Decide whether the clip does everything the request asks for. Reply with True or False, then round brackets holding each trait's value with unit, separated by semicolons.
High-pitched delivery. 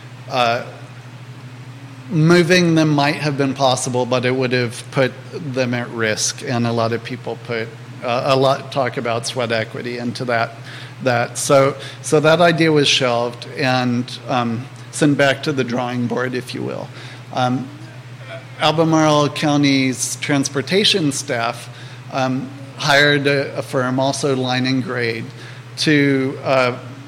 False (130 Hz)